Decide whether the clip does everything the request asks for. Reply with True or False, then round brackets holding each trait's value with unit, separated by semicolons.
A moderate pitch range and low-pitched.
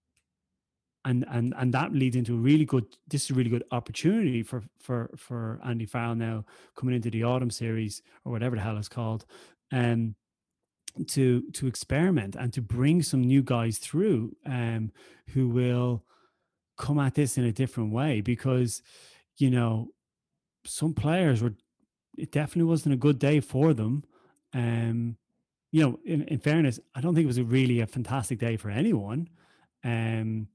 True (3.7 semitones; 125 Hz)